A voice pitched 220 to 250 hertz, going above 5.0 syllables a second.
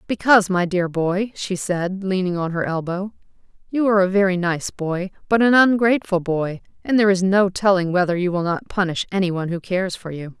No: medium, 185 Hz; 5.6 syllables/s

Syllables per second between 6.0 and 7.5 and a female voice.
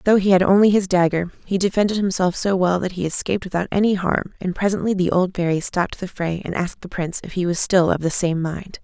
Yes: 6.2 syllables/s; female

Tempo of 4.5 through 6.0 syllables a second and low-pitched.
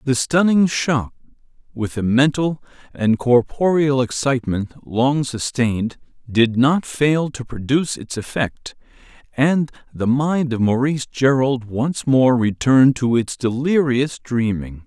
No: 4.0 syllables/s; low, 130 Hz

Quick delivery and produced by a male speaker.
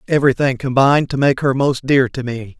Yes: fast, 210 wpm; male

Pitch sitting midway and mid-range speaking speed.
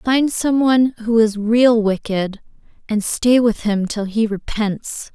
No: high, 225 Hz; average, 165 wpm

